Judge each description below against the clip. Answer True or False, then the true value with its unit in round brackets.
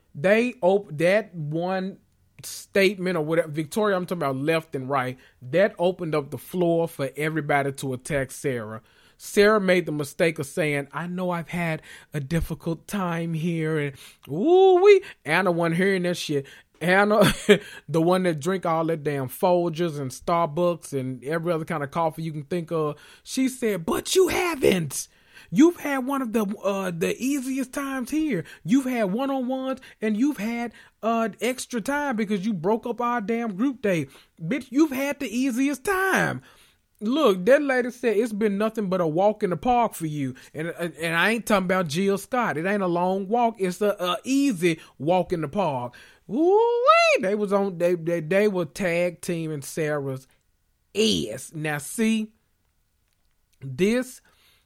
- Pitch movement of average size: False (6.1 semitones)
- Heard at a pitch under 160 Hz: False (185 Hz)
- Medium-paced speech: True (175 wpm)